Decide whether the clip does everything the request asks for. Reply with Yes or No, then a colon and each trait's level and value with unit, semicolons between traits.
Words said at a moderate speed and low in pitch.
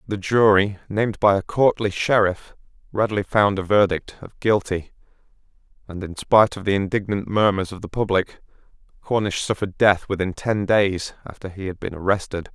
Yes: average, 165 wpm; low, 100 Hz